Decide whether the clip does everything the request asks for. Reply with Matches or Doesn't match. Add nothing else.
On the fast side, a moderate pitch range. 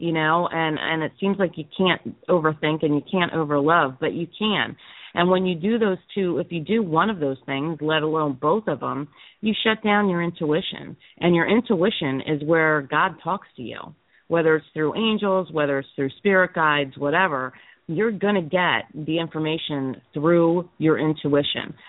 Doesn't match